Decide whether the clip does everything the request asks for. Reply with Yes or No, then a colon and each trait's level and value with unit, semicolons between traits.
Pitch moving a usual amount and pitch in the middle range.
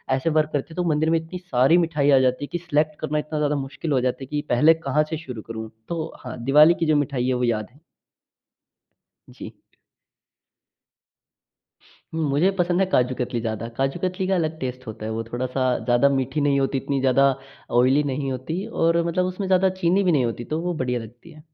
Yes: average, 4.3 semitones; medium, 145 Hz